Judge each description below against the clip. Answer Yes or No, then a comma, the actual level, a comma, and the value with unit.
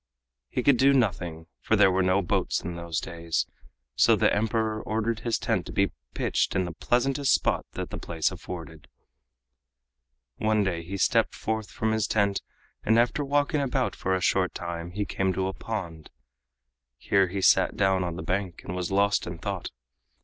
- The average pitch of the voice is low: Yes, very low, 95 Hz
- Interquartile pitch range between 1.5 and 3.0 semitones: No, average, 4.1 semitones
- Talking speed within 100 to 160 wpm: No, average, 185 wpm